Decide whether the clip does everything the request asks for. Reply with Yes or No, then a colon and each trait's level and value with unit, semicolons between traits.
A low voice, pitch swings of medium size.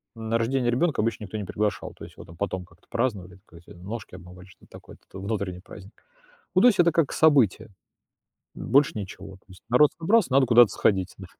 No: low, 110 Hz; wide, 5.7 semitones